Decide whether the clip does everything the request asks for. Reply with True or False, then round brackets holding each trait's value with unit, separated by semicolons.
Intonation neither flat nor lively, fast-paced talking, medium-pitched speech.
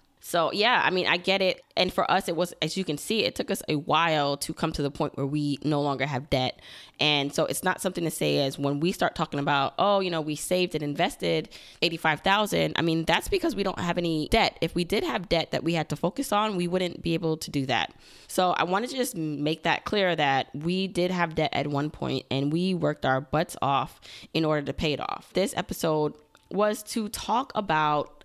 True (3.8 semitones; 245 wpm; 160 Hz)